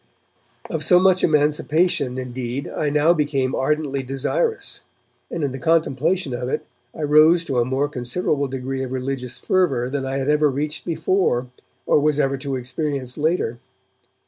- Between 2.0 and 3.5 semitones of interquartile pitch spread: Yes, average, 3.0 semitones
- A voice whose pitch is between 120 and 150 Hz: Yes, medium, 140 Hz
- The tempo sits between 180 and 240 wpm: No, average, 160 wpm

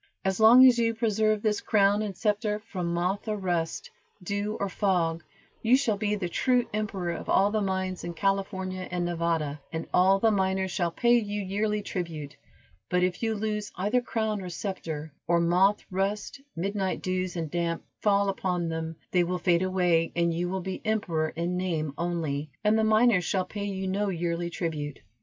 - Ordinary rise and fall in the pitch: Yes, average, 3.4 semitones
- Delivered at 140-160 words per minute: No, average, 185 wpm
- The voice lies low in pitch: No, high, 190 Hz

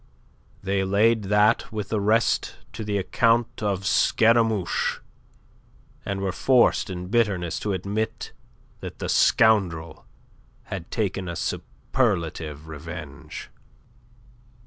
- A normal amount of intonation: Yes, average, 3.7 semitones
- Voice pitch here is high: No, low, 100 Hz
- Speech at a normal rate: No, slow, 105 wpm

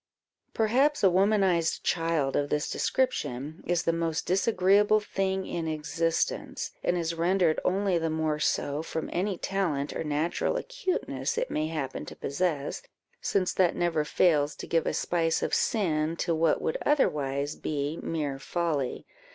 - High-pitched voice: No, medium, 165 Hz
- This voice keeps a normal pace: Yes, average, 150 wpm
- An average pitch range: Yes, average, 3.8 semitones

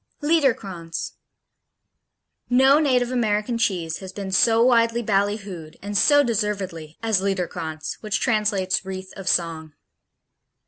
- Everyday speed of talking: No, slow, 110 wpm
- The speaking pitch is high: Yes, high, 205 Hz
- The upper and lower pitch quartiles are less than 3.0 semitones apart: No, average, 3.9 semitones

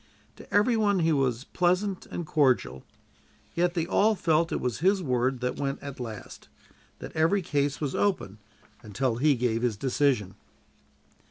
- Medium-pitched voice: Yes, medium, 145 Hz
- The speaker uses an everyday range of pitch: No, wide, 6.0 semitones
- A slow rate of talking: No, average, 160 wpm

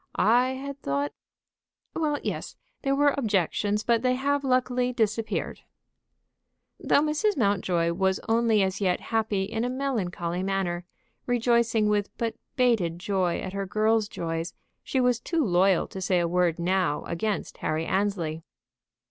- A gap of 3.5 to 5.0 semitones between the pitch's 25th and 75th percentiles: No, wide, 5.4 semitones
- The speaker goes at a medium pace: Yes, average, 150 wpm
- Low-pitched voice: No, high, 210 Hz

